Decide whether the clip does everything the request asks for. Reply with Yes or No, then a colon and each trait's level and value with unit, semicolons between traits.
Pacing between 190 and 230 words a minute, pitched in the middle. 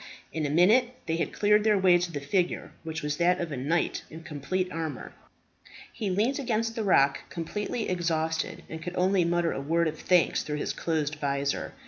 Yes: average, 195 wpm; medium, 170 Hz